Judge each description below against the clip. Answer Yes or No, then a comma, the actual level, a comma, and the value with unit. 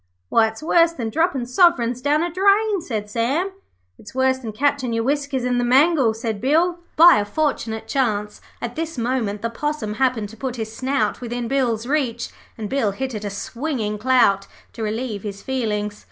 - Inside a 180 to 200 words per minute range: Yes, average, 185 wpm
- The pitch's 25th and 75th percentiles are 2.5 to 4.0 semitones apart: No, average, 4.5 semitones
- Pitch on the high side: Yes, high, 245 Hz